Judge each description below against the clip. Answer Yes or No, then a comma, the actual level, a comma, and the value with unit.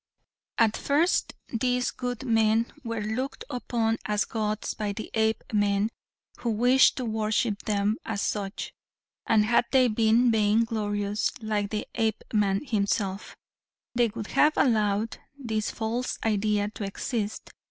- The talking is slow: Yes, slow, 130 wpm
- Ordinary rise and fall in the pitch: No, narrow, 2.0 semitones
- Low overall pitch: No, high, 220 Hz